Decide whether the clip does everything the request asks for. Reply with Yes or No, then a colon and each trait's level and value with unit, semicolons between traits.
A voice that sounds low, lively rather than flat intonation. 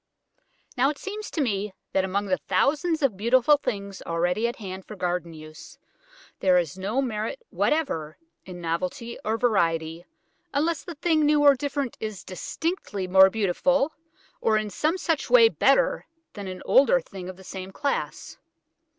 No: high, 215 Hz; wide, 7.6 semitones